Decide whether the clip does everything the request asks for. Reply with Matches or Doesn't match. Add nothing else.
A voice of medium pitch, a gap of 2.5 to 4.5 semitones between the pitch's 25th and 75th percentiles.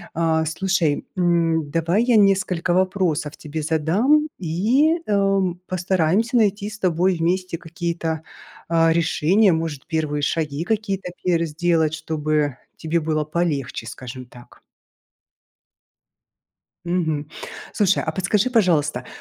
Matches